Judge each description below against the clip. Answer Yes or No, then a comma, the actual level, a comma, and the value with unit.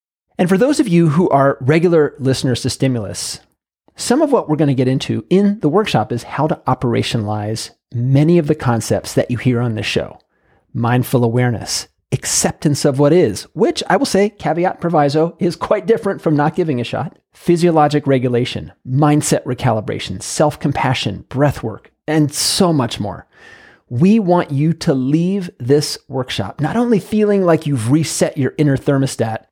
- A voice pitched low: No, medium, 145 Hz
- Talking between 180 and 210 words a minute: No, average, 170 wpm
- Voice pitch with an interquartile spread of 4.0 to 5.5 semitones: Yes, average, 5.1 semitones